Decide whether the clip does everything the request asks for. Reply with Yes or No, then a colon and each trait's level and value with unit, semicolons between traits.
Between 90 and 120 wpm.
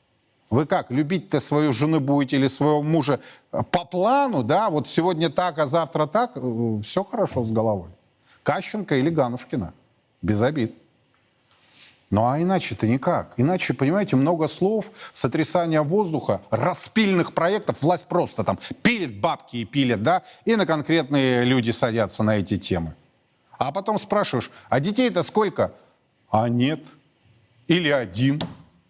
No: average, 135 wpm